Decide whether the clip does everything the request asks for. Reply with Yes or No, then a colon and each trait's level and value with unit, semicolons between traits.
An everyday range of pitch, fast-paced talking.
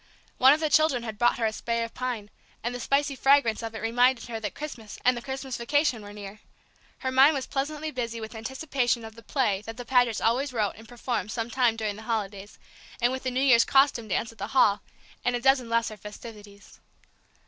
Yes: average, 3.0 semitones; fast, 220 wpm